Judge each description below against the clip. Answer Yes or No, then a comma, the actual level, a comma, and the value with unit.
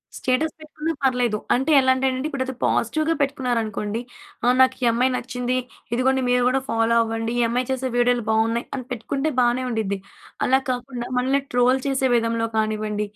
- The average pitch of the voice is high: Yes, very high, 250 Hz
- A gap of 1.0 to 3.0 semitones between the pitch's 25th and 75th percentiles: Yes, narrow, 2.4 semitones